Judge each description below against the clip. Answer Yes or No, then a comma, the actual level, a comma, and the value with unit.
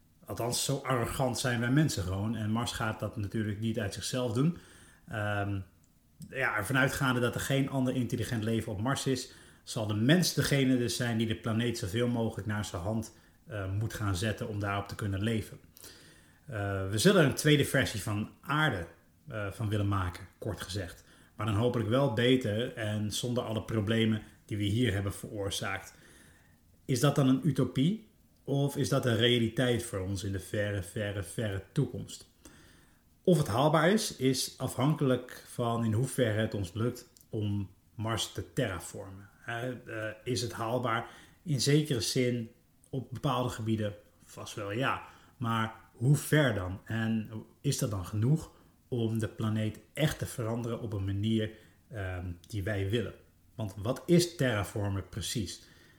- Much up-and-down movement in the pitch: No, average, 3.9 semitones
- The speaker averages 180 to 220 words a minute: No, average, 160 wpm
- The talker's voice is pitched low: Yes, low, 115 Hz